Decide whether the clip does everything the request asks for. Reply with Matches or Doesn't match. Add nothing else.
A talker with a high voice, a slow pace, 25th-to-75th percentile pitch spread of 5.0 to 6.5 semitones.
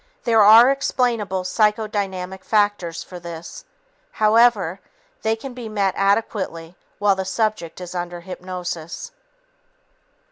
Doesn't match